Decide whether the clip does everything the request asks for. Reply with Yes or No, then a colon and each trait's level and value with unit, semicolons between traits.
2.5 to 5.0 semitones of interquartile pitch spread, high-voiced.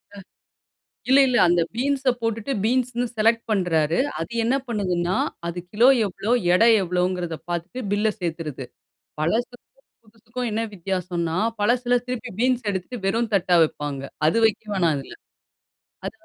No: wide, 5.5 semitones; high, 210 Hz